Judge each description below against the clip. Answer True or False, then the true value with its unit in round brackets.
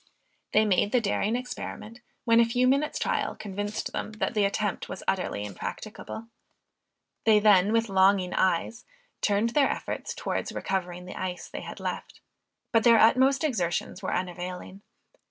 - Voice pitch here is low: False (210 Hz)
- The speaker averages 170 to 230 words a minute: False (155 wpm)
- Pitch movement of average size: True (3.6 semitones)